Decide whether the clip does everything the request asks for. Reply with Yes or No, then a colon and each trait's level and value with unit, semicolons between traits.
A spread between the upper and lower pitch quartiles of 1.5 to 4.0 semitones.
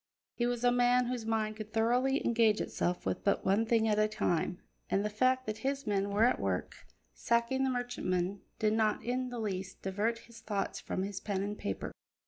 Yes: average, 3.3 semitones